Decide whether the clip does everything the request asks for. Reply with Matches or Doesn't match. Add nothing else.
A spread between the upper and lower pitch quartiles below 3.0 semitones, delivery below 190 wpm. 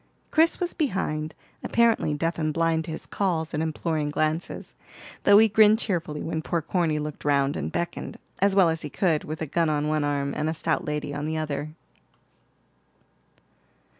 Matches